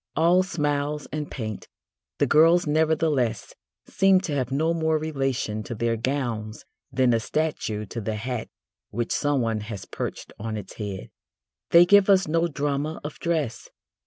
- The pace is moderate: Yes, average, 155 wpm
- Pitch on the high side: No, medium, 140 Hz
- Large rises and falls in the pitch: Yes, wide, 5.9 semitones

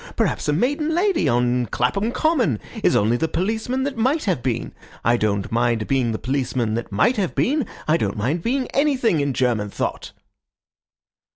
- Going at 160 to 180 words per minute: Yes, average, 175 wpm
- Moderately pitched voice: Yes, medium, 145 Hz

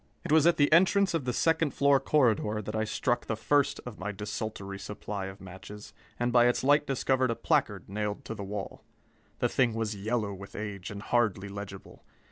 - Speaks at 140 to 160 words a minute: No, average, 200 wpm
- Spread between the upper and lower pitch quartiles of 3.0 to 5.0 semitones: Yes, average, 4.5 semitones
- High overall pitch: No, low, 110 Hz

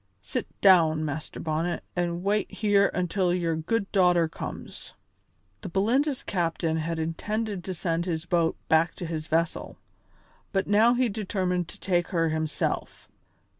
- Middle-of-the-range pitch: Yes, medium, 175 Hz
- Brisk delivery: No, average, 145 wpm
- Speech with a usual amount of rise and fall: Yes, average, 3.4 semitones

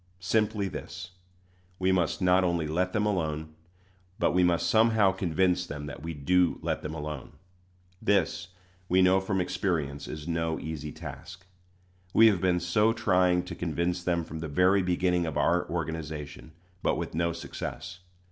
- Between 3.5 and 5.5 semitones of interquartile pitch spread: No, narrow, 2.5 semitones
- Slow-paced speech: No, average, 160 wpm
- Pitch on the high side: No, very low, 90 Hz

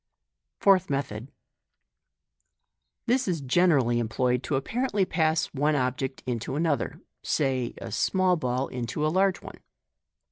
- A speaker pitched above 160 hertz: No, medium, 140 Hz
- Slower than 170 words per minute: Yes, slow, 135 wpm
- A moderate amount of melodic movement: No, wide, 5.9 semitones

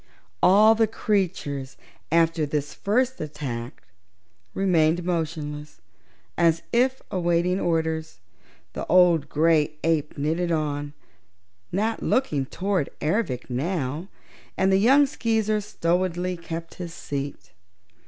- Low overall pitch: No, medium, 170 Hz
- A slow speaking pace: Yes, slow, 105 wpm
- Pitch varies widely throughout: No, average, 4.2 semitones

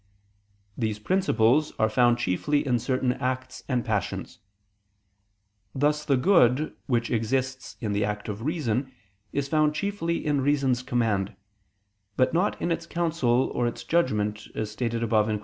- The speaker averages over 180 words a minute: No, average, 150 wpm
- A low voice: Yes, low, 125 Hz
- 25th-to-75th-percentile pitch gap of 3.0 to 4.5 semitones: No, average, 5.0 semitones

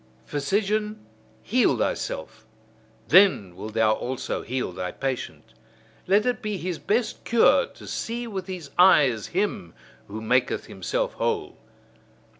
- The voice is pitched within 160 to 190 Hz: Yes, medium, 185 Hz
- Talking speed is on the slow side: Yes, slow, 125 wpm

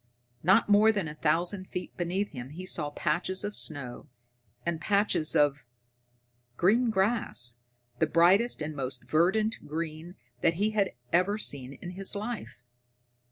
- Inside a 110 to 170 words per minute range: Yes, average, 145 wpm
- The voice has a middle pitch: Yes, medium, 175 Hz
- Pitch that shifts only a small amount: No, average, 5.0 semitones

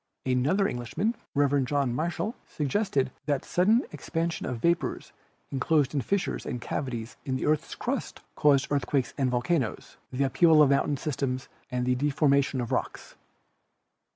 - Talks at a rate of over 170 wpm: No, average, 155 wpm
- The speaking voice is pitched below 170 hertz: Yes, medium, 140 Hz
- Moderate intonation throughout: Yes, average, 3.4 semitones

